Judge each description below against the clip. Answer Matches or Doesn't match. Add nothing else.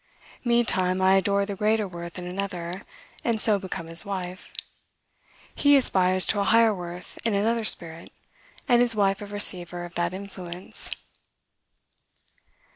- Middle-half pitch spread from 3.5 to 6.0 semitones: Doesn't match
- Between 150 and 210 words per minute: Doesn't match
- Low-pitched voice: Doesn't match